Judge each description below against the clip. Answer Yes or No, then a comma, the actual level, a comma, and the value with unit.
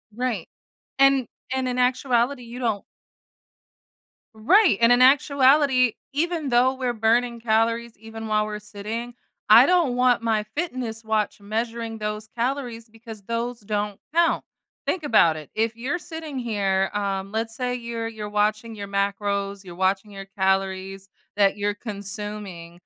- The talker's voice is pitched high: Yes, high, 225 Hz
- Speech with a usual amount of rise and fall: Yes, average, 3.3 semitones